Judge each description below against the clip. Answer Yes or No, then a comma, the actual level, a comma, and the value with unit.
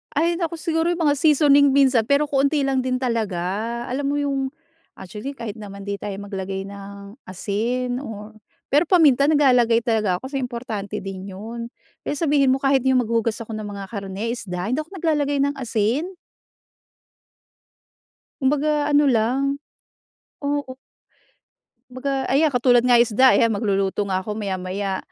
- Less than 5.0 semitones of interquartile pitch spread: No, wide, 5.5 semitones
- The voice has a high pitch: Yes, high, 245 Hz